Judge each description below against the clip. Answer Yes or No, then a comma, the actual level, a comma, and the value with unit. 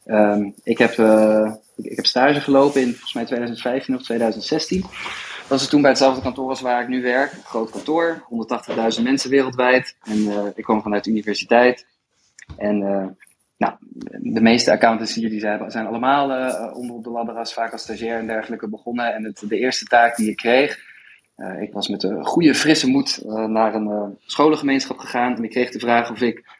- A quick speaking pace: Yes, fast, 210 wpm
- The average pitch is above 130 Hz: No, low, 120 Hz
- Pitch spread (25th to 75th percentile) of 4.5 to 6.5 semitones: No, average, 2.9 semitones